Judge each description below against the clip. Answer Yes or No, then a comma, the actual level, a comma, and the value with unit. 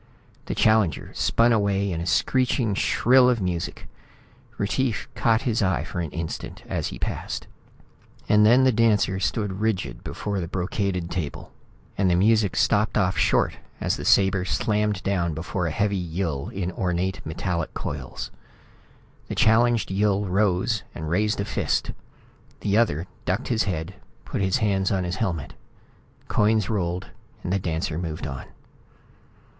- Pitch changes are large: No, average, 3.3 semitones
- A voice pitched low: Yes, very low, 95 Hz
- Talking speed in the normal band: Yes, average, 150 wpm